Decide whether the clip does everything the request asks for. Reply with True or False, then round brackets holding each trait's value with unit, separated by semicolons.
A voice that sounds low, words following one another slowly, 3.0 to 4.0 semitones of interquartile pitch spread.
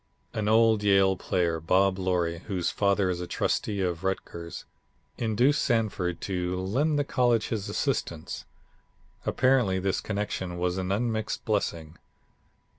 True (95 Hz; 130 wpm; 3.5 semitones)